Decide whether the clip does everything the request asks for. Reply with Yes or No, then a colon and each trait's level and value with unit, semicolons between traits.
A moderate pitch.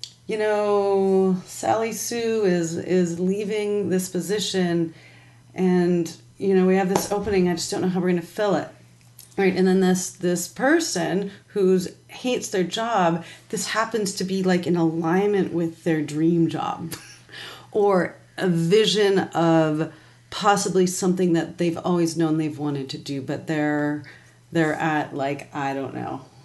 Yes: medium, 180 Hz